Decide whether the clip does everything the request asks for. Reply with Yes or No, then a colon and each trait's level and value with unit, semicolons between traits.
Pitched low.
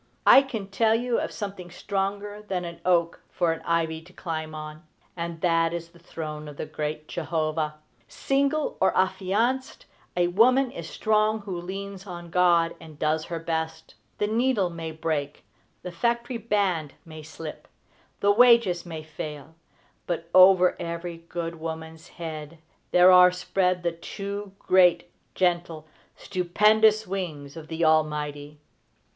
No: medium, 175 Hz